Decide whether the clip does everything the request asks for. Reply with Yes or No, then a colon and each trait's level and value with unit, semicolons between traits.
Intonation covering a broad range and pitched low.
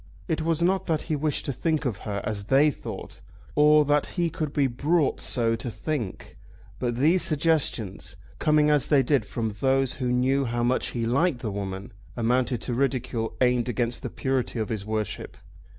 No: average, 4.5 semitones; low, 130 Hz